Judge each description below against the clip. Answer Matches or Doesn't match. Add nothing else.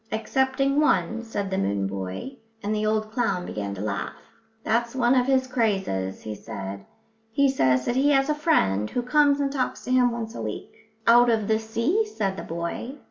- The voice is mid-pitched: Doesn't match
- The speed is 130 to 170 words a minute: Doesn't match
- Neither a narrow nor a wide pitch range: Doesn't match